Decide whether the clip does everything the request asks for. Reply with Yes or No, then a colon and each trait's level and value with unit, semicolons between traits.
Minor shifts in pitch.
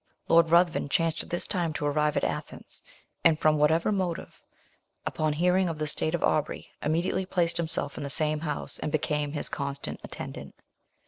Yes: narrow, 2.1 semitones